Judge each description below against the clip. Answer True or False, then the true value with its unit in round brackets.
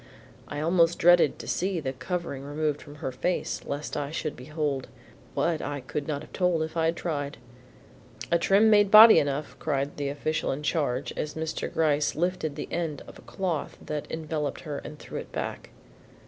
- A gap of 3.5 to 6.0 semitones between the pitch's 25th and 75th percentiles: False (2.9 semitones)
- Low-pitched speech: False (155 Hz)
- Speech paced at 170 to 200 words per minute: True (190 wpm)